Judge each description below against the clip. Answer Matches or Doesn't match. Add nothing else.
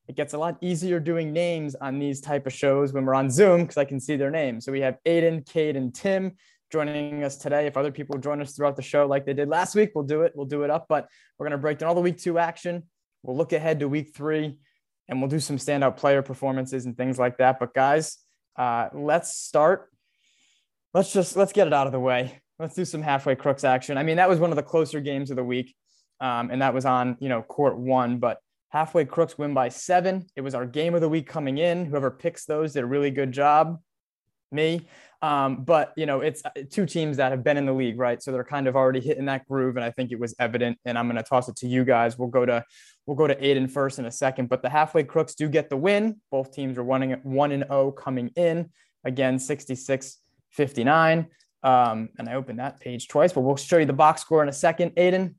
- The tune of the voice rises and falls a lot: Doesn't match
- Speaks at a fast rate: Matches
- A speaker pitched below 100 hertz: Doesn't match